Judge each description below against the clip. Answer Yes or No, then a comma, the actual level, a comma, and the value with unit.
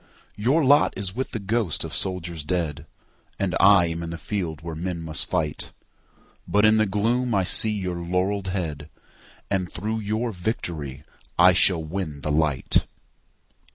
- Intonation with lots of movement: No, average, 4.1 semitones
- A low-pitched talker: Yes, very low, 90 Hz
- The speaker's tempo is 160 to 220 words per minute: No, average, 150 wpm